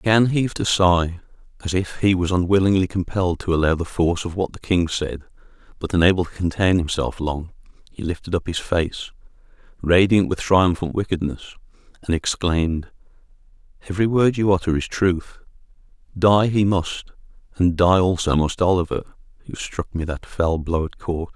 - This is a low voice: Yes, very low, 90 Hz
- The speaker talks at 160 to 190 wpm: Yes, average, 165 wpm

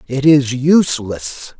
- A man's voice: Yes, male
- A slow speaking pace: Yes, slow, 115 wpm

